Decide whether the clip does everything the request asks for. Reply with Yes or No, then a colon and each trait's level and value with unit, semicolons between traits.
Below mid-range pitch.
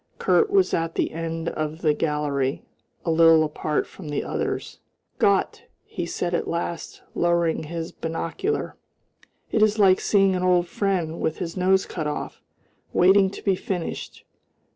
No: medium, 170 Hz